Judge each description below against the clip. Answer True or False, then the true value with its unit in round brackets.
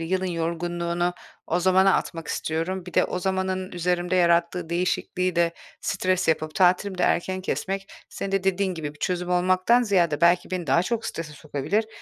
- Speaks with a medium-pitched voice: True (180 Hz)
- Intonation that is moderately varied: False (1.7 semitones)